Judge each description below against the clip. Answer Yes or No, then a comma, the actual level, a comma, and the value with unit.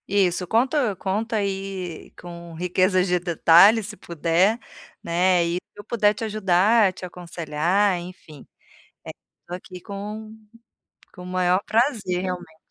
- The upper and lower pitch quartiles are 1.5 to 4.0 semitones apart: Yes, average, 2.8 semitones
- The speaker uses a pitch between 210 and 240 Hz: No, medium, 185 Hz